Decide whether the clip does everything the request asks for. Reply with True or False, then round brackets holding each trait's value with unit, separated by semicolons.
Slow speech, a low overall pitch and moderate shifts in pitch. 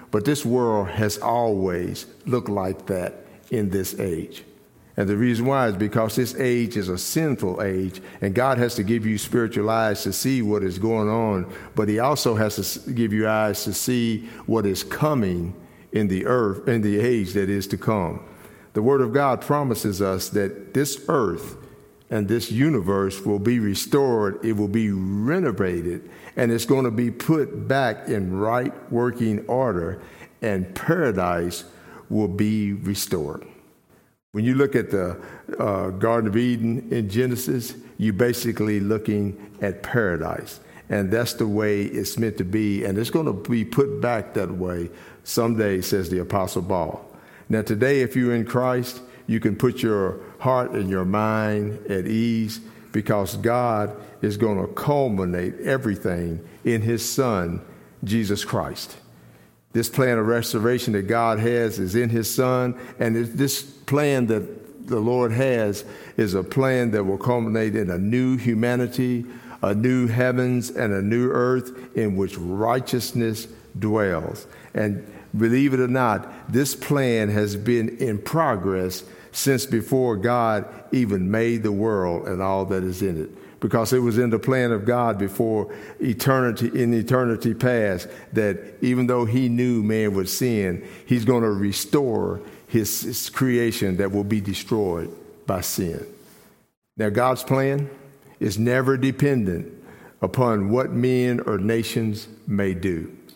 False (155 wpm; 110 Hz; 3.5 semitones)